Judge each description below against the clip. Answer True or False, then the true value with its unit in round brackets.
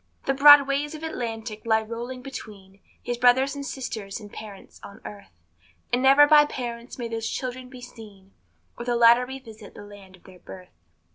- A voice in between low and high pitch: False (235 Hz)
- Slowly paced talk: False (185 wpm)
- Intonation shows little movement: False (3.8 semitones)